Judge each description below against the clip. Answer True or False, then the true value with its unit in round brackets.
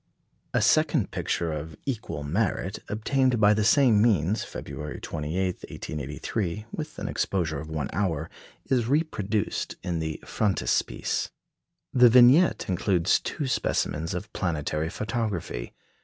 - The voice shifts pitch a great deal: True (6.3 semitones)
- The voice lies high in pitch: False (95 Hz)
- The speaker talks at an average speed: False (125 wpm)